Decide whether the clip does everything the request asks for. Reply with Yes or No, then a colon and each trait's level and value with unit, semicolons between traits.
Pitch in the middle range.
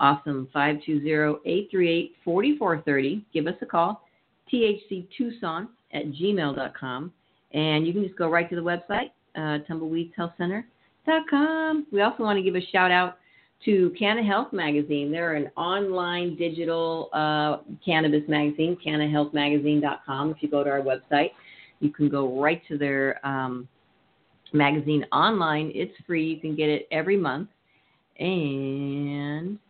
Yes: medium, 160 Hz